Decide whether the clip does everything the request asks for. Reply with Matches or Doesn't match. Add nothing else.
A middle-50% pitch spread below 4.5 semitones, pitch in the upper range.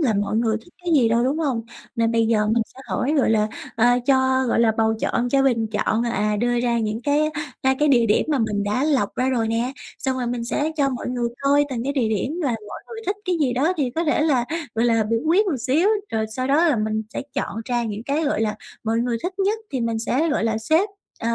Matches